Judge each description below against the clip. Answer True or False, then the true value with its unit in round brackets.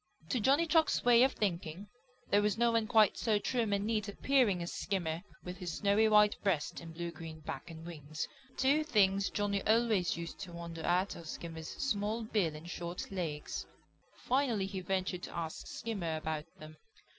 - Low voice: False (195 Hz)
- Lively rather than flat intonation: False (4.5 semitones)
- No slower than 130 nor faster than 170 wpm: False (180 wpm)